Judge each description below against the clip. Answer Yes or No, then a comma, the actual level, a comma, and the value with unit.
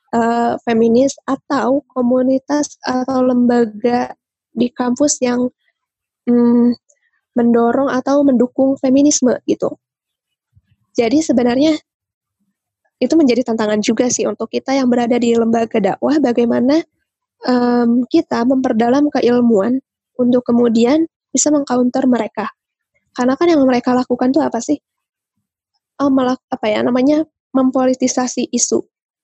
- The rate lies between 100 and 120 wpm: Yes, average, 110 wpm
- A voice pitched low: No, very high, 250 Hz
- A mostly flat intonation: Yes, narrow, 2.2 semitones